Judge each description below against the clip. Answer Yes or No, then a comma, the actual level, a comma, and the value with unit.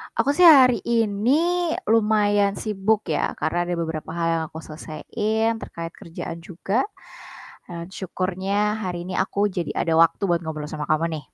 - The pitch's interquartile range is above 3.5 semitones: Yes, average, 4.5 semitones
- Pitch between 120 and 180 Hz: No, high, 190 Hz